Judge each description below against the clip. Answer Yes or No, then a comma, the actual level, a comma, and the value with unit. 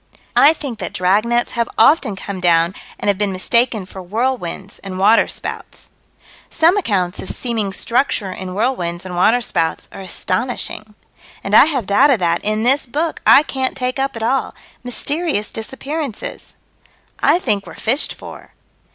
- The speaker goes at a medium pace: Yes, average, 150 wpm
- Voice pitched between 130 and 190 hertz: No, high, 220 Hz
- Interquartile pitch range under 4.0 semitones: No, wide, 5.5 semitones